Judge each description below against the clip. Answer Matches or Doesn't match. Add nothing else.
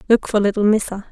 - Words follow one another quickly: Matches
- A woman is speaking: Matches